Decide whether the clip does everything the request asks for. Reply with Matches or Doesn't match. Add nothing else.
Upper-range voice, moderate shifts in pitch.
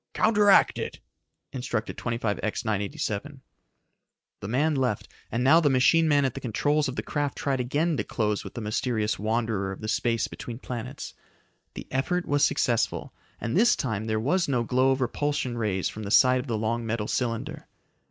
Doesn't match